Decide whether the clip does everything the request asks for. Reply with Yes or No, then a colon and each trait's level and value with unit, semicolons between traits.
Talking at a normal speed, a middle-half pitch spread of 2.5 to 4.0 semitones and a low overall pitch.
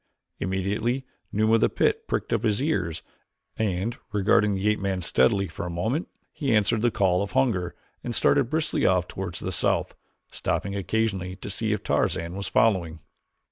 Yes: average, 175 wpm; average, 3.4 semitones; low, 100 Hz